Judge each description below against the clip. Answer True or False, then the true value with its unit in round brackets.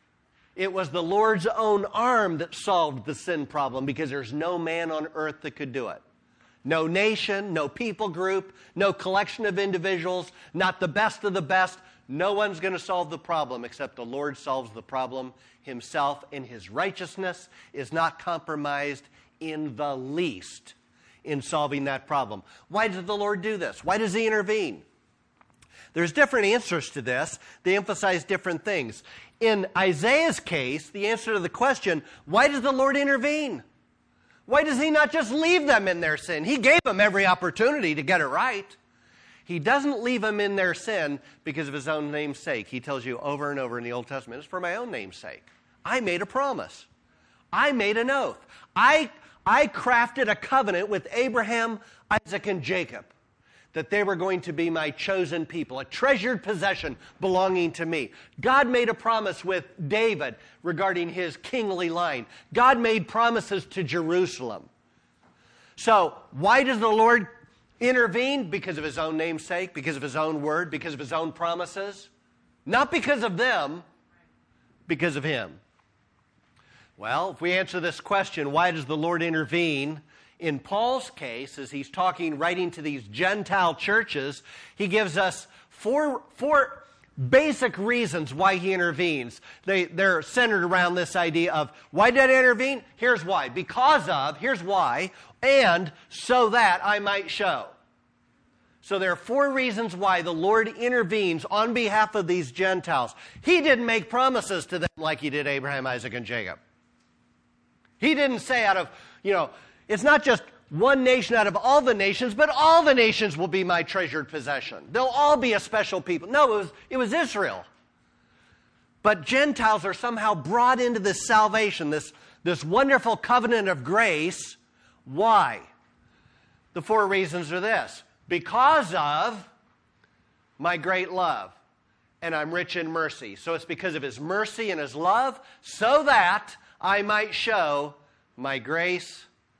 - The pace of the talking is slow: False (165 wpm)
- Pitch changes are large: True (6.2 semitones)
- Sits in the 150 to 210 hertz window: True (185 Hz)